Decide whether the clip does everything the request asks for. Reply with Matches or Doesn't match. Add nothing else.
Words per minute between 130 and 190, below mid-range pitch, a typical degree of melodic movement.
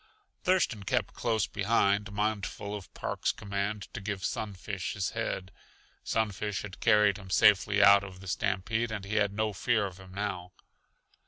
Doesn't match